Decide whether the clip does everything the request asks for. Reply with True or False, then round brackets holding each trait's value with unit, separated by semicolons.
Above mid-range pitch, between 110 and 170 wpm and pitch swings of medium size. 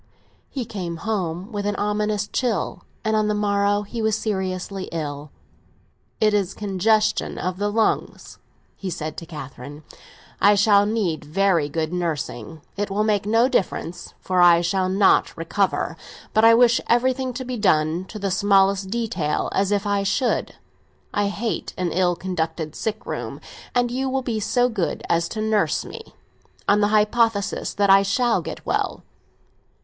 True (200 Hz; 165 wpm; 3.5 semitones)